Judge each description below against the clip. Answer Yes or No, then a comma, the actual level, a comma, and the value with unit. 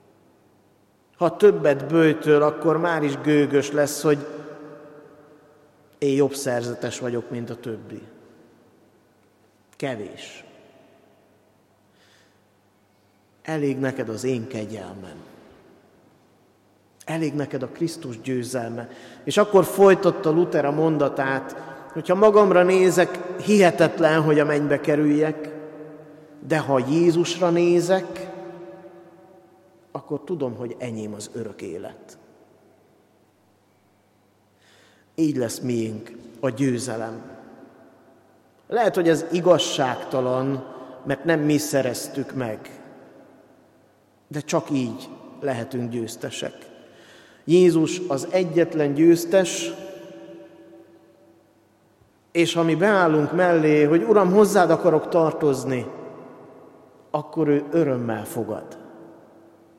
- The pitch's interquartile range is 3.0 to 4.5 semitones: No, wide, 5.5 semitones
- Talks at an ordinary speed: No, slow, 90 wpm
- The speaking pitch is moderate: Yes, medium, 145 Hz